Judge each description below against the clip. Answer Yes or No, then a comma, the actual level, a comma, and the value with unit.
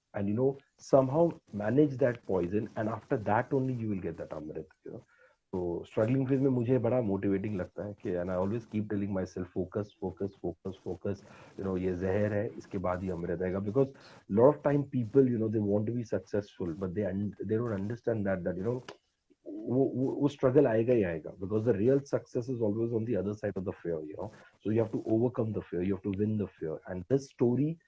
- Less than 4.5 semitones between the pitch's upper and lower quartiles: No, average, 4.8 semitones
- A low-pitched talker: Yes, low, 105 Hz